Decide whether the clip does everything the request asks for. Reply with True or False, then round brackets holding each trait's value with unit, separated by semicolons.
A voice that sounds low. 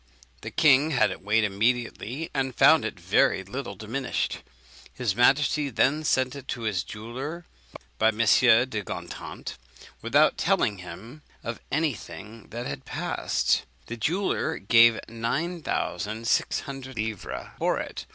True (120 Hz)